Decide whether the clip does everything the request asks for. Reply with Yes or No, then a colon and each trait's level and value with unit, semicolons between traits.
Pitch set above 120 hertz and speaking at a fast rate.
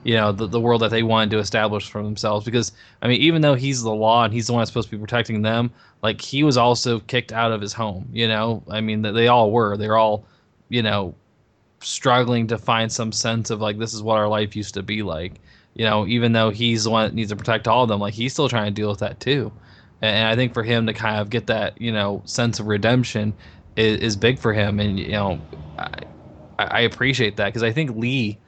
No: low, 110 Hz; fast, 255 wpm